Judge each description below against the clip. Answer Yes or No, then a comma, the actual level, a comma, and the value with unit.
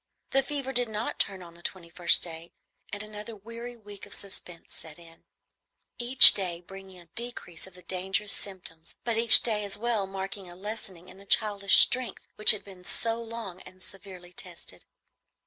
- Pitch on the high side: Yes, high, 195 Hz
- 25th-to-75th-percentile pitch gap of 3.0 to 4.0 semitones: Yes, average, 3.6 semitones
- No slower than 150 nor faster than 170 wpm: No, average, 180 wpm